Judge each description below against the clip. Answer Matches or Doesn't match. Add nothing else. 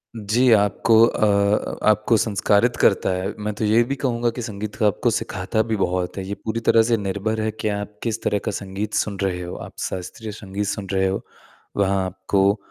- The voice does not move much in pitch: Matches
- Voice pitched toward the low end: Matches